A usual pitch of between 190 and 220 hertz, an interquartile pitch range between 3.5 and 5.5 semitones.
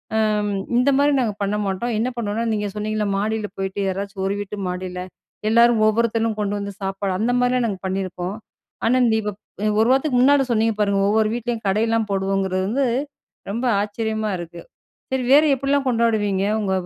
No: high, 215 Hz; average, 3.0 semitones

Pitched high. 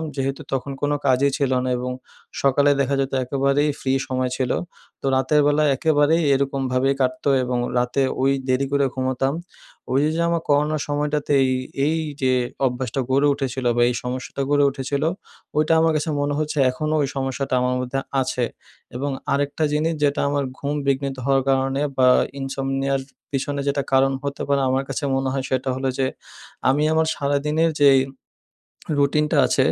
No: medium, 140 Hz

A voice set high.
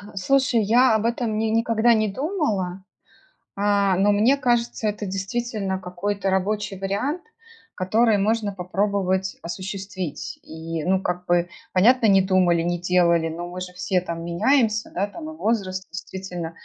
Yes: high, 195 Hz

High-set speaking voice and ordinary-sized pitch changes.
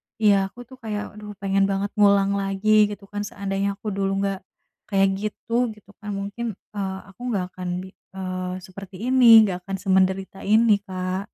No: high, 200 Hz; narrow, 1.5 semitones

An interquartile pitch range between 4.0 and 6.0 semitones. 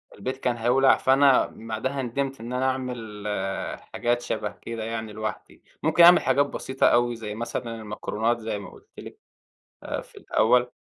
No: average, 3.0 semitones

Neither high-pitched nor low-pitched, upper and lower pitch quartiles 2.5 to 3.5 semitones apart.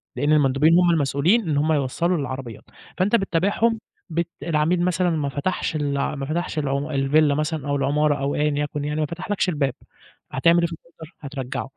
Yes: medium, 150 Hz; average, 3.2 semitones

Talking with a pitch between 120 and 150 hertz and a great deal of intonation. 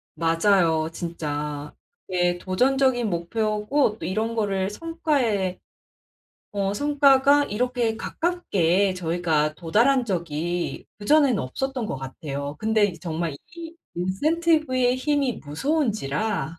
No: high, 205 Hz; wide, 7.7 semitones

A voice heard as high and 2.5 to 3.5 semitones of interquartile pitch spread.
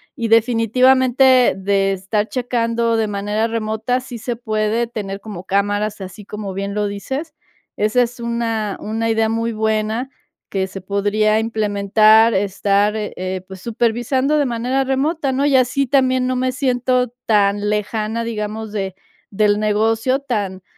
Yes: high, 220 Hz; average, 3.1 semitones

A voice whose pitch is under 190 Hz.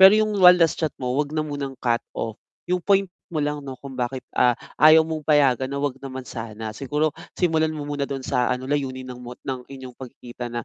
Yes: low, 135 Hz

